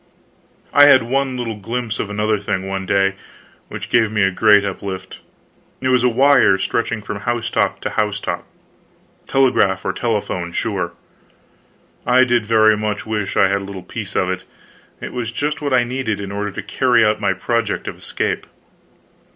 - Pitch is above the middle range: No, low, 110 Hz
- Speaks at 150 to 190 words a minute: Yes, average, 175 wpm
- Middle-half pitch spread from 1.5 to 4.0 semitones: Yes, average, 3.4 semitones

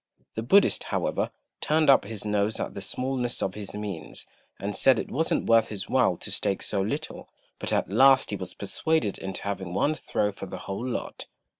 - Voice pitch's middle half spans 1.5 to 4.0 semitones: No, average, 5.0 semitones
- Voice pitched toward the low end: Yes, low, 105 Hz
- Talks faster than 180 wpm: Yes, average, 195 wpm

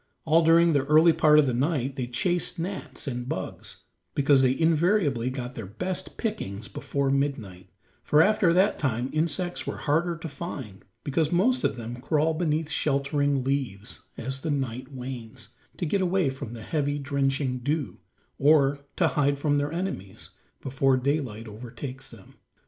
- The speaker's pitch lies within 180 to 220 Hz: No, medium, 140 Hz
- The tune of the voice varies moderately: Yes, average, 4.1 semitones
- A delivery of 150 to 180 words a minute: Yes, average, 160 wpm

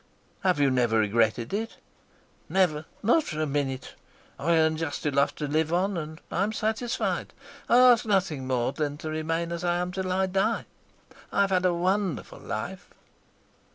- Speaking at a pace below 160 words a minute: No, average, 165 wpm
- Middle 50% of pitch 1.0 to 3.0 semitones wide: No, average, 4.8 semitones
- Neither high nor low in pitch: Yes, medium, 165 Hz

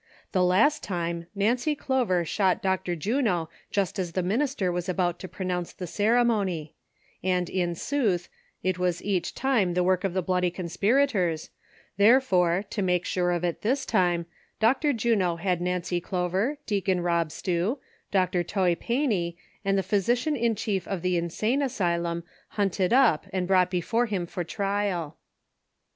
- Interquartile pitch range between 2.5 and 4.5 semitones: Yes, average, 3.4 semitones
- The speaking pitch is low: No, medium, 185 Hz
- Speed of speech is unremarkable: Yes, average, 155 wpm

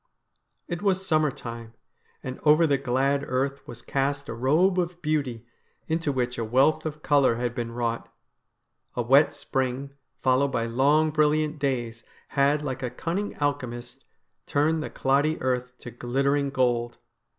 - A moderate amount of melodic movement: Yes, average, 3.6 semitones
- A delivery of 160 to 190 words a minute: No, average, 150 wpm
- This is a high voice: No, low, 135 Hz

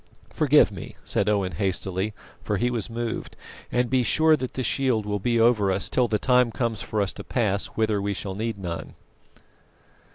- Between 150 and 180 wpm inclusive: No, average, 190 wpm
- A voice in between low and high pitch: No, low, 110 Hz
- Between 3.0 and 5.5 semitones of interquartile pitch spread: Yes, average, 3.4 semitones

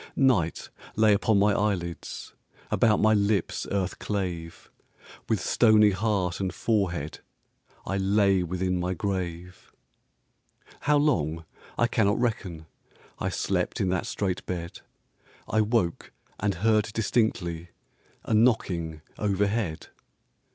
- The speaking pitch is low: Yes, low, 100 Hz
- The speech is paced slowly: Yes, slow, 115 wpm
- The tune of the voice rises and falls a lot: No, average, 3.5 semitones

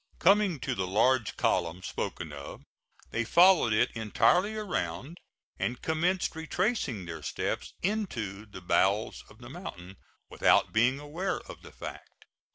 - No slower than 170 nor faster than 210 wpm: No, average, 140 wpm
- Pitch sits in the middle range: No, low, 120 Hz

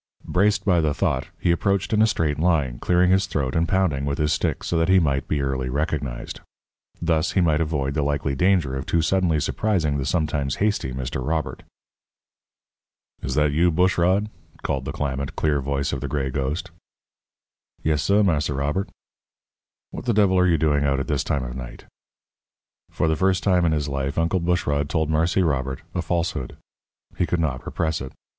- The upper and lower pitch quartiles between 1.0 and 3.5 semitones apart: No, average, 4.3 semitones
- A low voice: Yes, very low, 80 Hz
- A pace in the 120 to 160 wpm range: No, average, 190 wpm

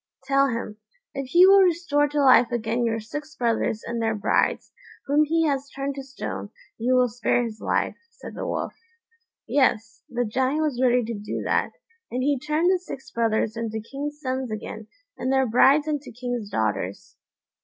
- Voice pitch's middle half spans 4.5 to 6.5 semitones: No, average, 4.1 semitones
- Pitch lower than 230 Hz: No, very high, 255 Hz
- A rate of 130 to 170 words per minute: No, average, 180 wpm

